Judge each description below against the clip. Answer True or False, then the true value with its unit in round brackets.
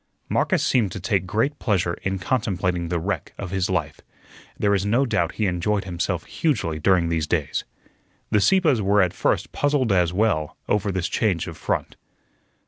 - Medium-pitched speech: False (95 Hz)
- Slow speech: False (175 wpm)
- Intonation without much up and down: False (3.4 semitones)